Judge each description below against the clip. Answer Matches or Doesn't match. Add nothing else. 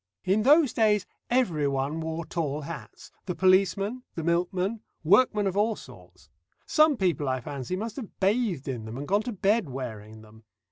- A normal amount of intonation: Doesn't match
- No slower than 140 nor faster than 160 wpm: Doesn't match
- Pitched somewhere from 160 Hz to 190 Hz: Matches